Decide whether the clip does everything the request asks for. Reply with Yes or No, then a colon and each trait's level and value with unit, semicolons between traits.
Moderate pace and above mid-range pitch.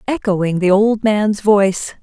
Yes: average, 150 wpm; high, 205 Hz